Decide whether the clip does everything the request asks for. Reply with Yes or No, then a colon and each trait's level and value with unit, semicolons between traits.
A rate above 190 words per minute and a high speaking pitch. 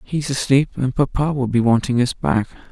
No: average, 200 wpm; low, 125 Hz